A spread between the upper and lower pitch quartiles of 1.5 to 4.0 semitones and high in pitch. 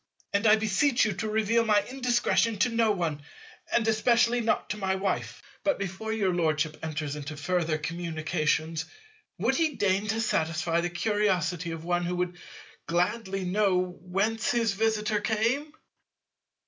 No: average, 4.4 semitones; high, 195 Hz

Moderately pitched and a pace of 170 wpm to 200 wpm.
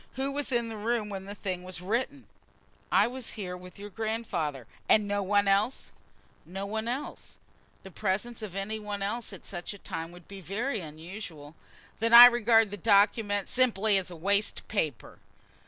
No: high, 205 Hz; average, 175 wpm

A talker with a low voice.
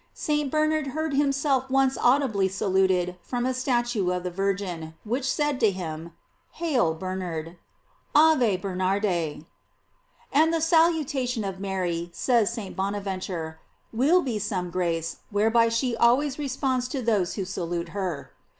No: high, 210 Hz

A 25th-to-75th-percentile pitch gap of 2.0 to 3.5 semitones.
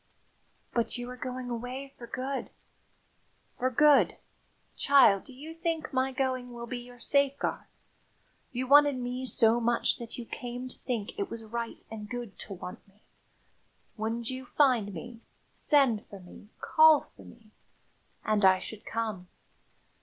Yes: average, 2.8 semitones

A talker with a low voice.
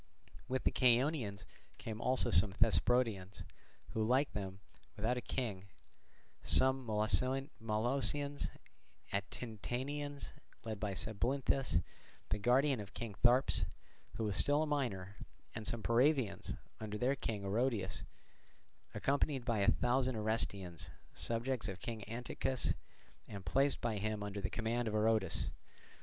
Yes: low, 115 Hz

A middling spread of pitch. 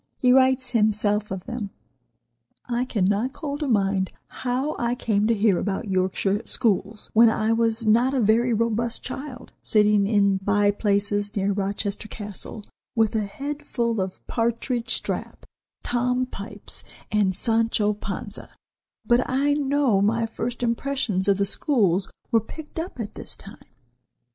Yes: average, 3.3 semitones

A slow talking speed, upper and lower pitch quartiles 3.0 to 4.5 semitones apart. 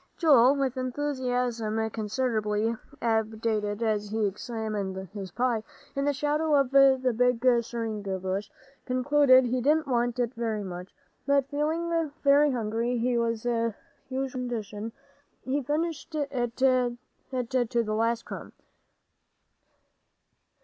Yes: slow, 120 wpm; average, 3.4 semitones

